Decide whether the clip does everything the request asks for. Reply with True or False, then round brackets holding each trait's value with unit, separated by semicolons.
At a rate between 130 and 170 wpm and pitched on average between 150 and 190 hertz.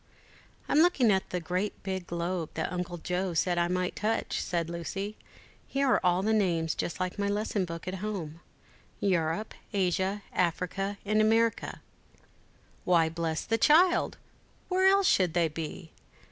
True (155 wpm; 185 Hz)